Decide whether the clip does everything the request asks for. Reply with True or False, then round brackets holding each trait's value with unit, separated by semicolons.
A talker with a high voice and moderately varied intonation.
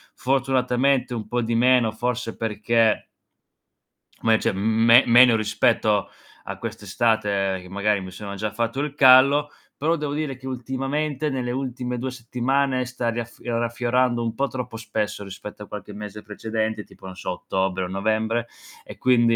False (120 Hz; 3.2 semitones)